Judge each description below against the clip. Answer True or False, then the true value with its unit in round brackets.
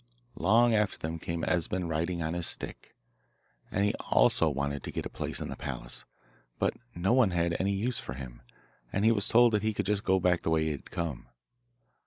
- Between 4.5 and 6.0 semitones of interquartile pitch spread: False (4.1 semitones)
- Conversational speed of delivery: False (215 wpm)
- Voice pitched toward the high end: False (90 Hz)